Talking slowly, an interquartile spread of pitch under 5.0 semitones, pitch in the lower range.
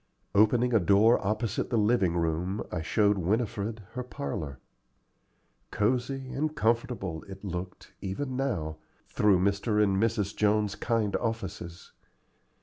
Yes: slow, 125 wpm; average, 3.6 semitones; low, 105 Hz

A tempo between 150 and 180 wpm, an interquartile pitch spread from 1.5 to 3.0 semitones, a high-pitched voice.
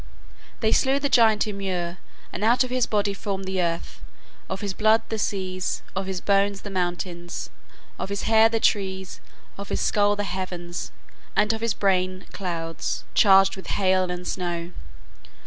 Yes: average, 165 wpm; narrow, 2.4 semitones; high, 195 Hz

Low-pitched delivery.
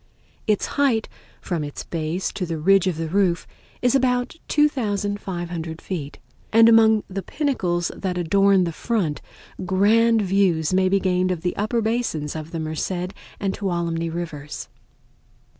No: medium, 185 Hz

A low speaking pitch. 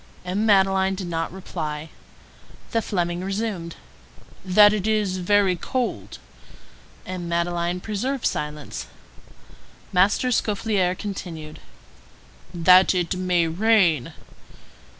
No: medium, 185 Hz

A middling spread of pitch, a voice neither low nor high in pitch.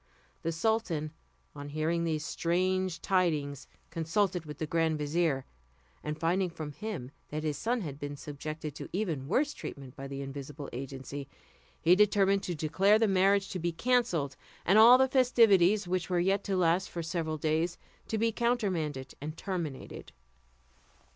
Yes: average, 4.6 semitones; medium, 170 Hz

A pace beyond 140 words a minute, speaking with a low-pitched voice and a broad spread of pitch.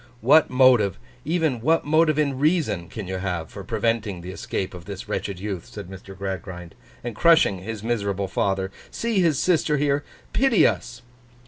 Yes: average, 155 wpm; low, 110 Hz; wide, 7.3 semitones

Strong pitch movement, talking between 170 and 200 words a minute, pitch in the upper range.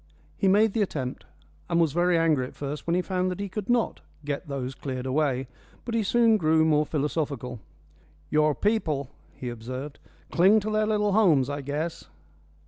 No: wide, 6.0 semitones; average, 180 wpm; medium, 160 Hz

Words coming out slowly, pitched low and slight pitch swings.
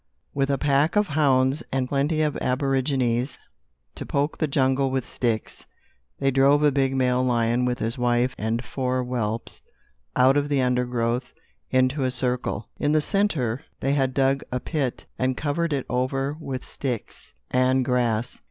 No: average, 160 wpm; low, 130 Hz; narrow, 1.9 semitones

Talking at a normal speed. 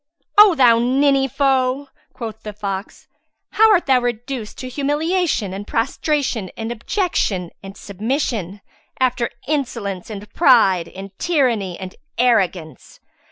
No: slow, 120 wpm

